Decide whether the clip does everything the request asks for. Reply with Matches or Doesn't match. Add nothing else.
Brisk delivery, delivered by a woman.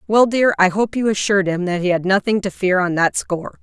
Matches